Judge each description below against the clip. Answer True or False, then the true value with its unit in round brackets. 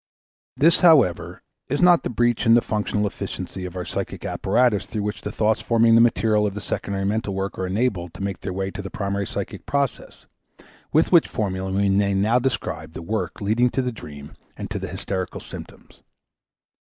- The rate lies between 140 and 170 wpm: False (195 wpm)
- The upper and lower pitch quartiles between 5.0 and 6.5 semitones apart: False (3.6 semitones)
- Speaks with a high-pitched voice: False (105 Hz)